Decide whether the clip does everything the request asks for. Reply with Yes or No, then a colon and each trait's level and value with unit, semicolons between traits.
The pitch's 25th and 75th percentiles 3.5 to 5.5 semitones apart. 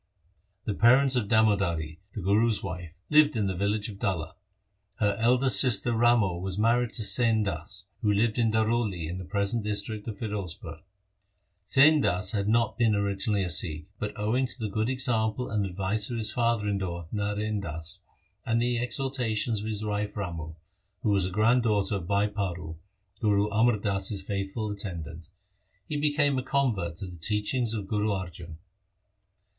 No: average, 3.1 semitones